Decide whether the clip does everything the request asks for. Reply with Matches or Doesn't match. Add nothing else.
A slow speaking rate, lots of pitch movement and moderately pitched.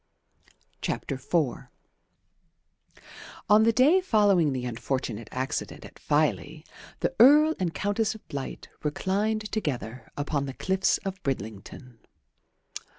Matches